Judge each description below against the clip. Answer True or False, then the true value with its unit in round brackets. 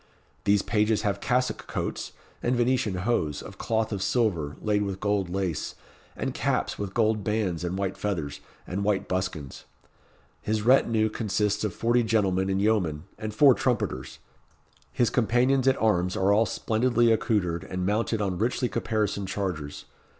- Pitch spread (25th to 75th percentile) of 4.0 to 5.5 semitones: False (3.2 semitones)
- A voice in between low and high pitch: False (105 Hz)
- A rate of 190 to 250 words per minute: False (155 wpm)